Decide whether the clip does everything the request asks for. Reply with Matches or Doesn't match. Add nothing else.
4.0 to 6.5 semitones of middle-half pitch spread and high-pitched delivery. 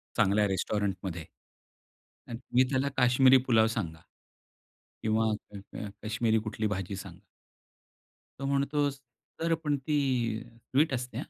Doesn't match